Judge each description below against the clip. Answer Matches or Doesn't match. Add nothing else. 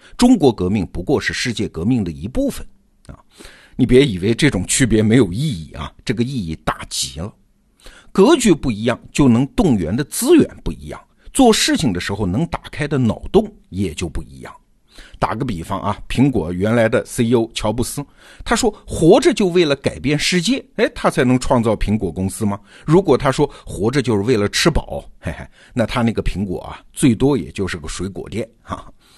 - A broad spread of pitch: Matches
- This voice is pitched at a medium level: Doesn't match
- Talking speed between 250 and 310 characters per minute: Matches